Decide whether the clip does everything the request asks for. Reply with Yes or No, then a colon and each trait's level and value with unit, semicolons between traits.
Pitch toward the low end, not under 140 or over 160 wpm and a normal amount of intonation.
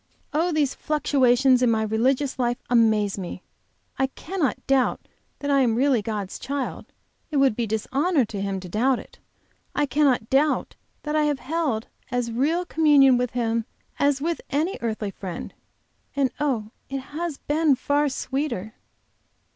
No: very high, 265 Hz; average, 155 wpm; average, 4.3 semitones